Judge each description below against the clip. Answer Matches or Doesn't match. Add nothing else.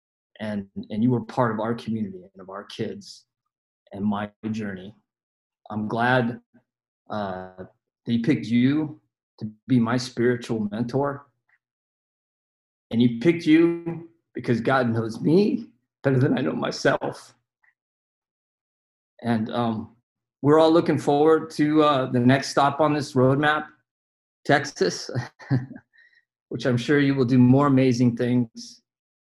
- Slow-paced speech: Matches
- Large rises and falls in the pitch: Doesn't match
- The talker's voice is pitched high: Doesn't match